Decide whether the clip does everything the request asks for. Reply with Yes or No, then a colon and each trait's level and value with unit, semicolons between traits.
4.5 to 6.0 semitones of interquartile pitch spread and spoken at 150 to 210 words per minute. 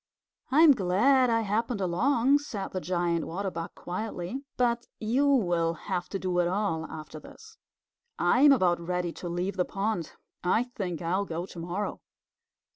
Yes: average, 5.2 semitones; average, 160 wpm